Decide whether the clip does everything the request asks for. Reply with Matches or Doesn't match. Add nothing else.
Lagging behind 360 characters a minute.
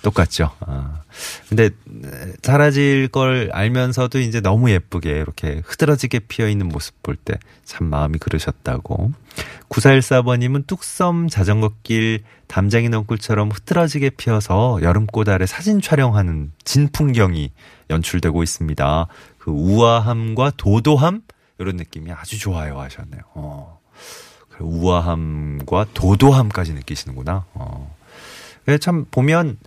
Matches